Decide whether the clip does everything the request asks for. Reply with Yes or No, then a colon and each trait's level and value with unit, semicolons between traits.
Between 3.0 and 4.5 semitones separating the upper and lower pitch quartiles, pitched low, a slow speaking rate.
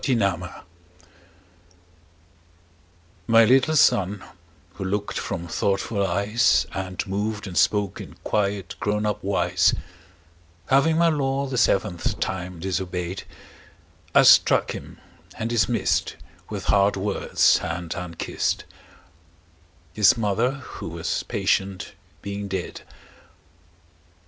Yes: average, 3.4 semitones; low, 100 Hz; slow, 110 wpm